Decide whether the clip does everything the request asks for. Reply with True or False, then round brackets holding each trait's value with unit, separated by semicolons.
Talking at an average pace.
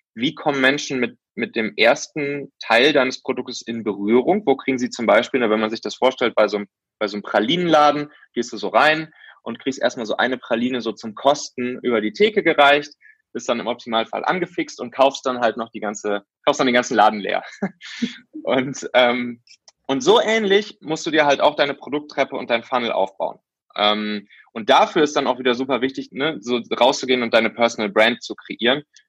False (200 wpm)